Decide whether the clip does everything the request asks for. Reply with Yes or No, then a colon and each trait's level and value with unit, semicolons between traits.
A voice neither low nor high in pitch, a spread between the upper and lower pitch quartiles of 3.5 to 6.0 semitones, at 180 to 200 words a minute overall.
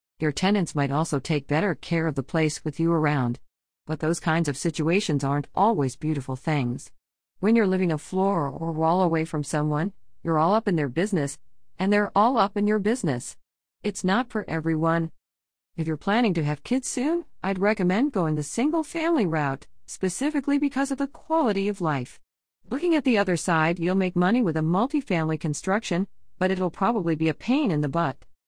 Yes: medium, 170 Hz; average, 5.2 semitones; average, 190 wpm